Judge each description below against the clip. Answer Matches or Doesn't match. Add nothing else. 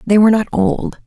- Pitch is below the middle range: Doesn't match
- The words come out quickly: Matches